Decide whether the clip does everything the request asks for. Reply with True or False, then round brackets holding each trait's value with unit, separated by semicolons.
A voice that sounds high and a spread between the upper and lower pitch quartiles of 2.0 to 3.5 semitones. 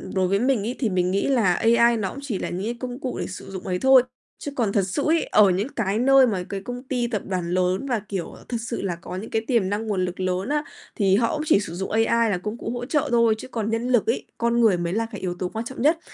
False (220 Hz; 4.4 semitones)